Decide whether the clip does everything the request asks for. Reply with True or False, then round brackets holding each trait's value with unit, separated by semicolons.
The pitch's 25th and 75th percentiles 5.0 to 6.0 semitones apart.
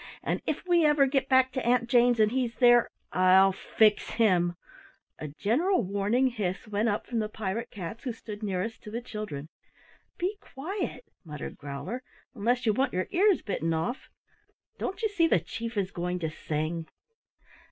True (5.6 semitones)